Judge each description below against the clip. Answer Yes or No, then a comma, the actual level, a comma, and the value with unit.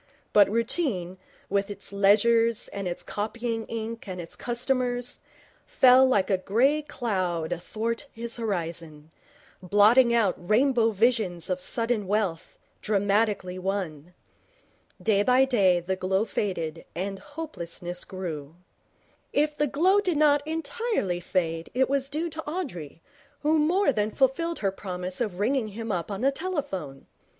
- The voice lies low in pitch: No, high, 210 Hz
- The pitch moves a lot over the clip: Yes, wide, 5.8 semitones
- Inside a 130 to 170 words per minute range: Yes, average, 140 wpm